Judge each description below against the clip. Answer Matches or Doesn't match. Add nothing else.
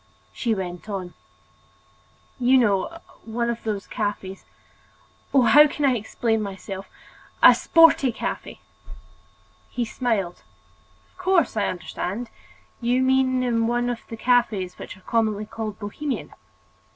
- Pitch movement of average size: Matches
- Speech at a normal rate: Doesn't match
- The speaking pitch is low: Doesn't match